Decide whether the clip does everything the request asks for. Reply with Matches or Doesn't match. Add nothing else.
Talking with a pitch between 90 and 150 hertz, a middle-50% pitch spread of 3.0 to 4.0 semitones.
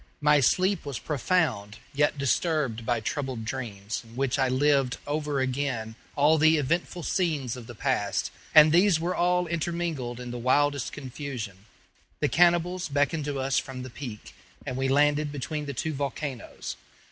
Matches